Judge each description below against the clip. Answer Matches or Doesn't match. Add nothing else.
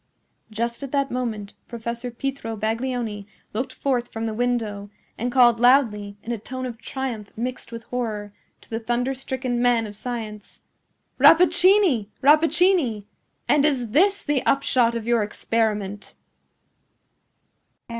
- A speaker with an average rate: Doesn't match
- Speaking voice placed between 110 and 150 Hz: Doesn't match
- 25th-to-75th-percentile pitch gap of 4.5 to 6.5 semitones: Doesn't match